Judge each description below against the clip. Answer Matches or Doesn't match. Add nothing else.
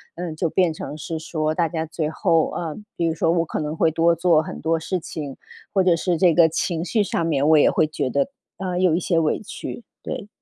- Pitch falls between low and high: Matches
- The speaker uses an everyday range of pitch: Doesn't match